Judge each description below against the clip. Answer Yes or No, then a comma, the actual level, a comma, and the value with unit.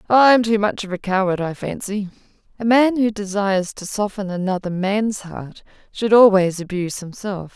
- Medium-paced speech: Yes, average, 165 wpm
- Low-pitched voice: No, high, 200 Hz